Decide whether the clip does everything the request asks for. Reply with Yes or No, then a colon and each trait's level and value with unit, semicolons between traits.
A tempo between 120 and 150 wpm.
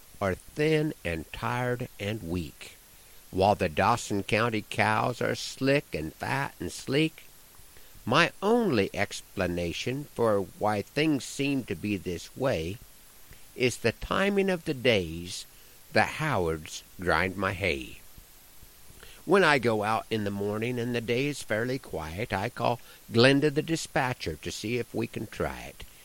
Yes: average, 145 wpm